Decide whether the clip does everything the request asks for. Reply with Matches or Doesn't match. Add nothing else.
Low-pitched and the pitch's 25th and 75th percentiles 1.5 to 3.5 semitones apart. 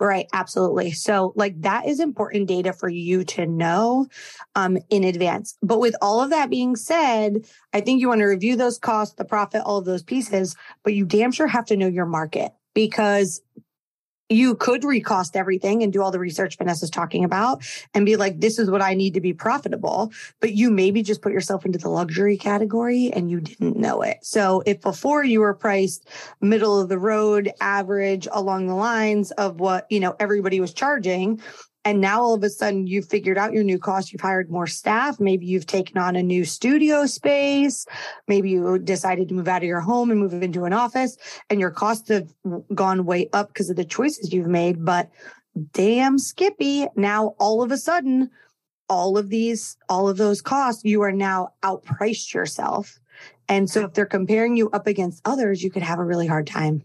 Doesn't match